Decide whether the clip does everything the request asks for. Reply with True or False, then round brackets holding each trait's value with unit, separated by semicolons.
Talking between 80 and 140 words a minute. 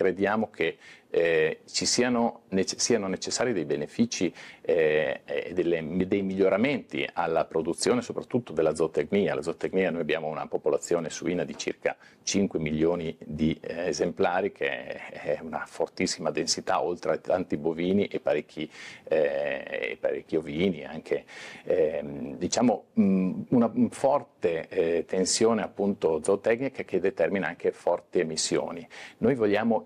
True (130 wpm)